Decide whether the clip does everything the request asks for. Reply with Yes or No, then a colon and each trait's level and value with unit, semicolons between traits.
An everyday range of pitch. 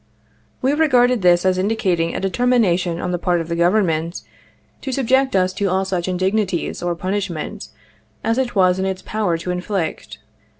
Yes: average, 3.7 semitones